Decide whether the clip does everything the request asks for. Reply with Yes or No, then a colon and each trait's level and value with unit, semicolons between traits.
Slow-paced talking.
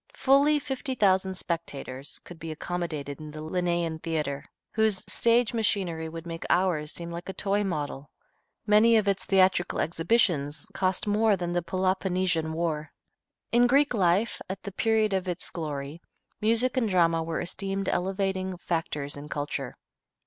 No: average, 155 wpm